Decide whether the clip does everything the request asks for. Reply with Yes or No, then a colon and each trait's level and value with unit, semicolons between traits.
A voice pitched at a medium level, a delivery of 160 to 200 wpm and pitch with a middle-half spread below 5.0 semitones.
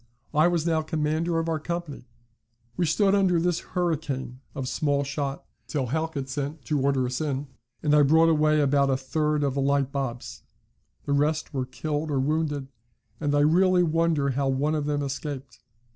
Yes: medium, 150 Hz; average, 180 wpm; narrow, 2.6 semitones